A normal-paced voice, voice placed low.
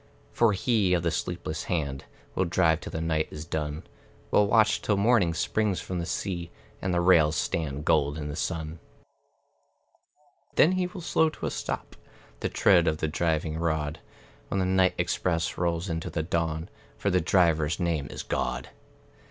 Yes: average, 175 wpm; very low, 85 Hz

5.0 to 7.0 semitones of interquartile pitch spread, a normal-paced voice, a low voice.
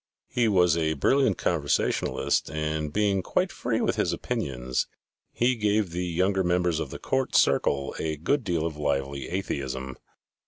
Yes: average, 5.3 semitones; average, 155 wpm; very low, 85 Hz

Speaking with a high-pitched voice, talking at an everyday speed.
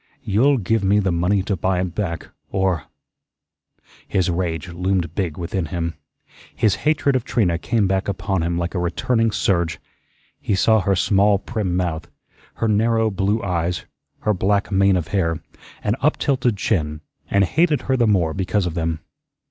No: very low, 95 Hz; average, 170 wpm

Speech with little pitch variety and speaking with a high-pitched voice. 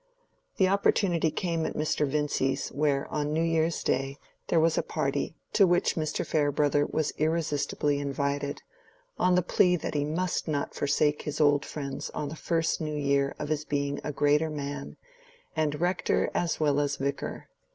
No: narrow, 2.1 semitones; medium, 150 Hz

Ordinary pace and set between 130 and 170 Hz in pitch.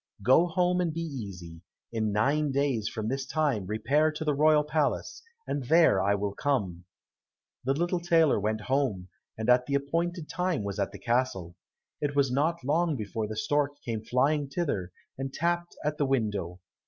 Yes: average, 180 wpm; low, 135 Hz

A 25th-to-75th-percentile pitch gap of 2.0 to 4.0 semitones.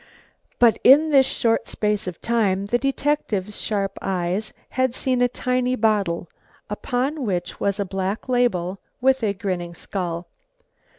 No: average, 4.9 semitones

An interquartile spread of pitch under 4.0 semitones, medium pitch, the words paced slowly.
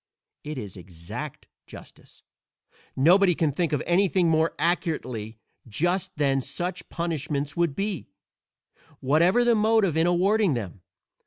No: average, 5.0 semitones; medium, 165 Hz; slow, 125 wpm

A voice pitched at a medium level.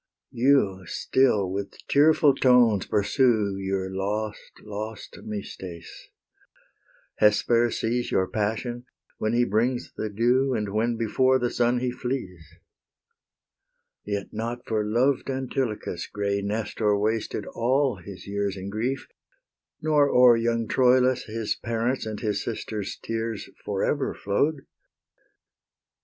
No: low, 115 Hz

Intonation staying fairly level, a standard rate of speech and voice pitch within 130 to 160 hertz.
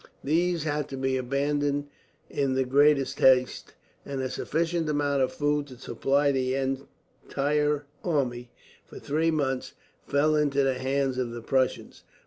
Yes: narrow, 2.0 semitones; average, 145 wpm; medium, 140 Hz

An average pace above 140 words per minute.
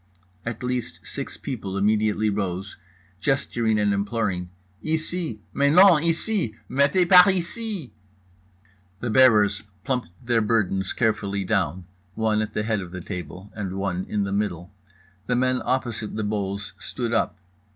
No: slow, 135 wpm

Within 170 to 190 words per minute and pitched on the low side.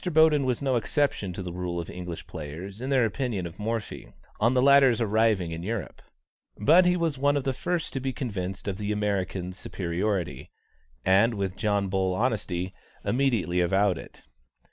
Yes: average, 175 wpm; low, 105 Hz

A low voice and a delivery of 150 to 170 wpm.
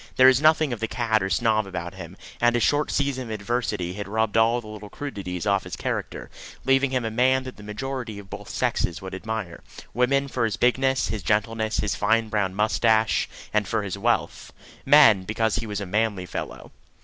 No: low, 110 Hz; fast, 205 wpm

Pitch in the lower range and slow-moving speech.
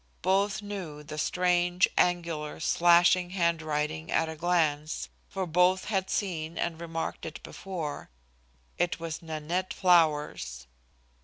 No: medium, 170 Hz; slow, 125 wpm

